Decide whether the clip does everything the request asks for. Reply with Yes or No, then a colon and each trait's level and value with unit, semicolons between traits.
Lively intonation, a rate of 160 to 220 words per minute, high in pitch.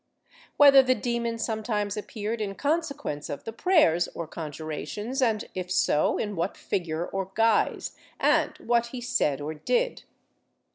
No: wide, 6.0 semitones; average, 150 wpm; high, 215 Hz